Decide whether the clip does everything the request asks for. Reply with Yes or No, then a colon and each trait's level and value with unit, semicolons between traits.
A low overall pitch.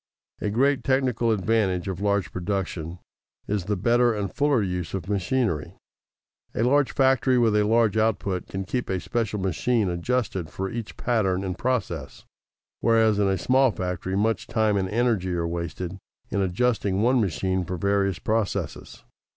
Yes: low, 105 Hz